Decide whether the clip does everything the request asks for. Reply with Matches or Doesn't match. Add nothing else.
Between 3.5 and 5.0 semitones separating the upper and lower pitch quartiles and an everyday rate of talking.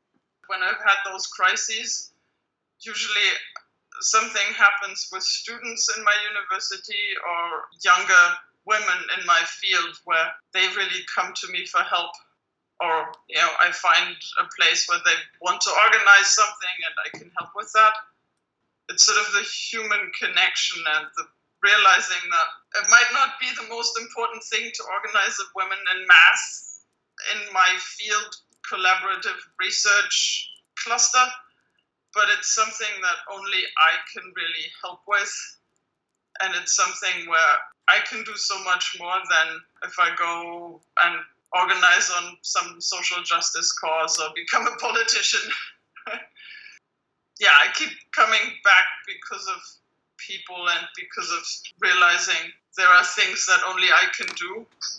Matches